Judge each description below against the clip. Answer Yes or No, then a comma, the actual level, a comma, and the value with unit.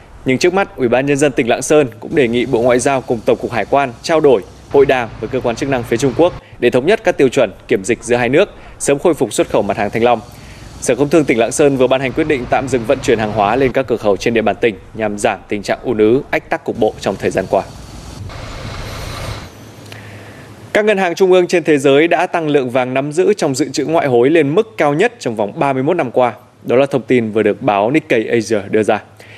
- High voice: No, low, 125 Hz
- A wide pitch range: No, average, 5.0 semitones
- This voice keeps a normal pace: No, fast, 270 wpm